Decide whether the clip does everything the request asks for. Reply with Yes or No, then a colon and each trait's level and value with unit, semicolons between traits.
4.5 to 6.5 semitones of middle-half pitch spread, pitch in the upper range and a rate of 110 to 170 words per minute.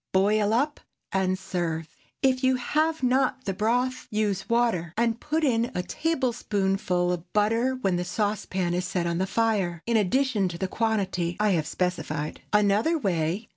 Yes: average, 5.1 semitones; high, 205 Hz; average, 165 wpm